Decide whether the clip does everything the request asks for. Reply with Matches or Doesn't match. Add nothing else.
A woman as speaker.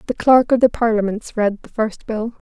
Matches